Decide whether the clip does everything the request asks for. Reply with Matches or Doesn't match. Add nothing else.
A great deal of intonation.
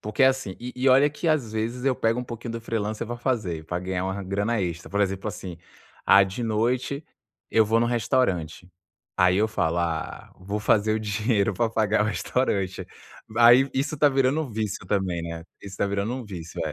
Doesn't match